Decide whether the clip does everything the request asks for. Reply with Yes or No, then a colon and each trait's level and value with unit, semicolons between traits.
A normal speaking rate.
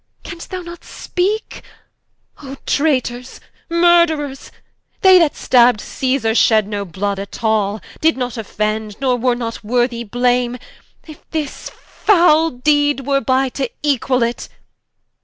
No: slow, 130 wpm